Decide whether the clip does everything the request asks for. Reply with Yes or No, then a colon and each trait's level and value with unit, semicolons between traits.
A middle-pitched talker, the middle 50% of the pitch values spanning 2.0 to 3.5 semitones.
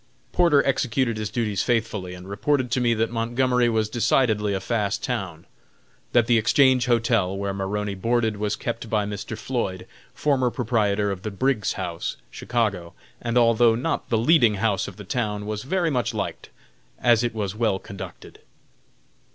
No: low, 115 Hz; average, 3.0 semitones